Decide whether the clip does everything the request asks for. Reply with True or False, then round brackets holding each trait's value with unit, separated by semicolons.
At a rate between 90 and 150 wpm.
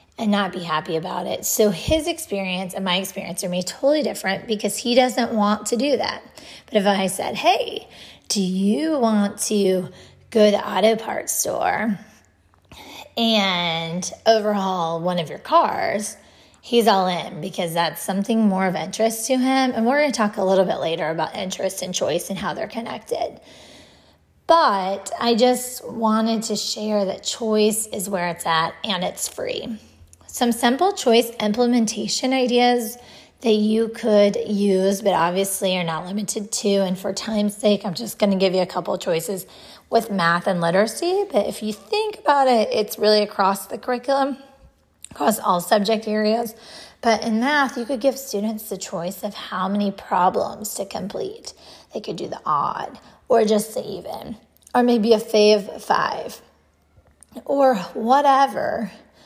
False (165 wpm)